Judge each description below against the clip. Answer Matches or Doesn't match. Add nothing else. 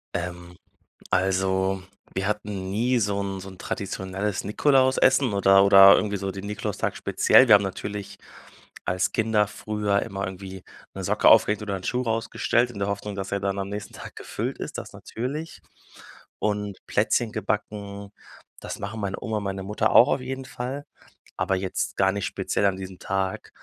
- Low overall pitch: Matches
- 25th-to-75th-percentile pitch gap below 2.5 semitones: Matches